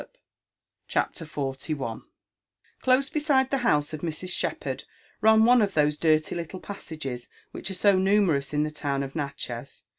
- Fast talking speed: No, average, 155 wpm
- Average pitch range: No, wide, 6.3 semitones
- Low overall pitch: No, medium, 160 Hz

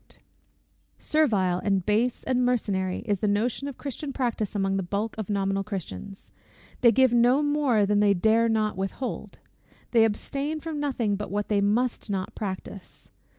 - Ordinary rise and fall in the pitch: Yes, average, 4.0 semitones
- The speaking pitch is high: Yes, high, 215 Hz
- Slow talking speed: No, average, 165 wpm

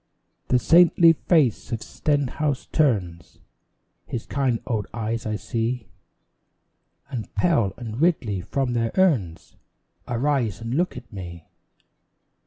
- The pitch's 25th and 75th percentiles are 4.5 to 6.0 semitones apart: Yes, average, 5.1 semitones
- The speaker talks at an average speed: No, slow, 115 wpm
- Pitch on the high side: No, low, 120 Hz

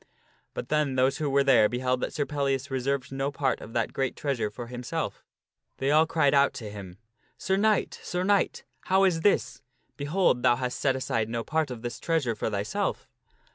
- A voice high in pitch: No, low, 135 Hz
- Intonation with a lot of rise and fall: No, average, 3.7 semitones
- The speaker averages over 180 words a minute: Yes, average, 200 wpm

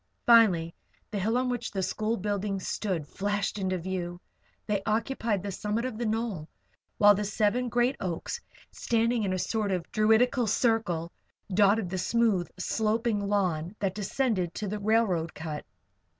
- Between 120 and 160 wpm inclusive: Yes, average, 155 wpm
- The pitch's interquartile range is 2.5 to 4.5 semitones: Yes, average, 3.3 semitones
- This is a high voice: Yes, high, 205 Hz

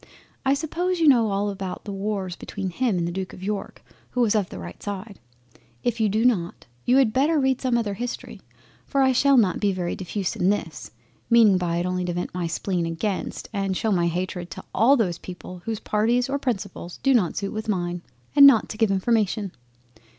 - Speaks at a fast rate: Yes, fast, 215 wpm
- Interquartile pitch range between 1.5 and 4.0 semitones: No, average, 4.7 semitones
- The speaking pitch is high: Yes, high, 205 Hz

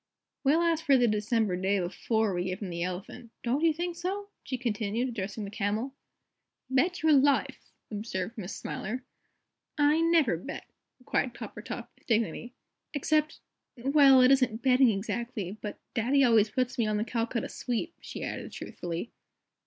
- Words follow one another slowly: No, average, 160 wpm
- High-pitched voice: Yes, high, 235 Hz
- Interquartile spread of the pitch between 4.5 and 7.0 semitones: Yes, average, 4.8 semitones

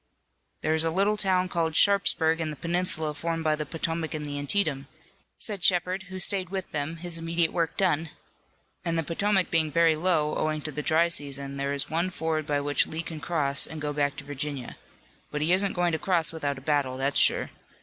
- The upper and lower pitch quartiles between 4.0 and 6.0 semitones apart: No, average, 2.9 semitones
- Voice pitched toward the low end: No, medium, 160 Hz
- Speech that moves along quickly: Yes, fast, 210 wpm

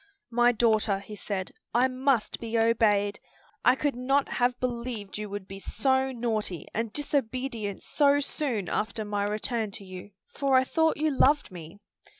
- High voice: Yes, high, 230 Hz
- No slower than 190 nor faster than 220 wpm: No, average, 160 wpm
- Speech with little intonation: No, average, 4.2 semitones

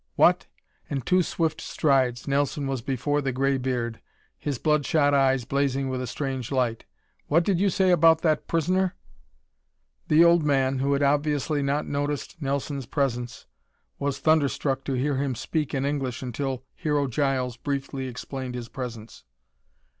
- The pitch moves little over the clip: Yes, narrow, 2.2 semitones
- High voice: No, medium, 140 Hz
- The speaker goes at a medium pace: Yes, average, 155 wpm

